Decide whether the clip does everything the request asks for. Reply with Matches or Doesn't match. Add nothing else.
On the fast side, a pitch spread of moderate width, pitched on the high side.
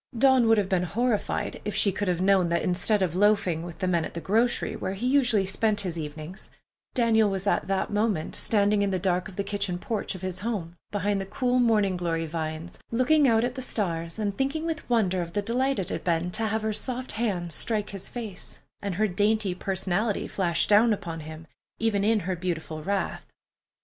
Matches